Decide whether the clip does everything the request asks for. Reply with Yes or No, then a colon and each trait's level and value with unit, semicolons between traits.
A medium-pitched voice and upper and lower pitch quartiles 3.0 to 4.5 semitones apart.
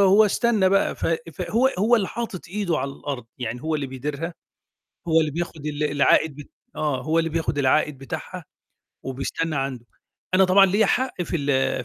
No: medium, 155 Hz; wide, 5.4 semitones